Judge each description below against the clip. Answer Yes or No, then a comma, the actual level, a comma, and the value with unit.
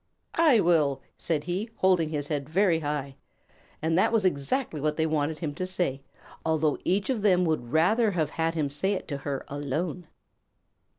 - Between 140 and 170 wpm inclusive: No, average, 180 wpm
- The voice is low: No, medium, 160 Hz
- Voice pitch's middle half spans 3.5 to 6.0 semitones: Yes, average, 4.1 semitones